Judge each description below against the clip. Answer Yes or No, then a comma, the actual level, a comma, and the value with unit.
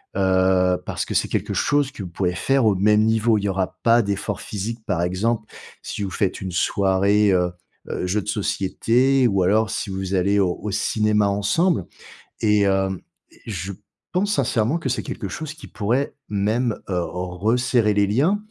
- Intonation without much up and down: No, average, 3.4 semitones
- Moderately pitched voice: No, low, 105 Hz